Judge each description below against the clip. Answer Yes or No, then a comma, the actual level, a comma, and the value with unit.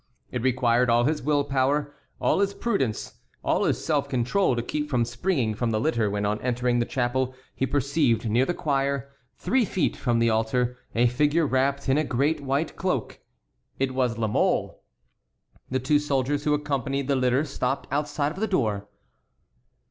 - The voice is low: Yes, low, 130 Hz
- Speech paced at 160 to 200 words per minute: Yes, average, 180 wpm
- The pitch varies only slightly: No, average, 3.4 semitones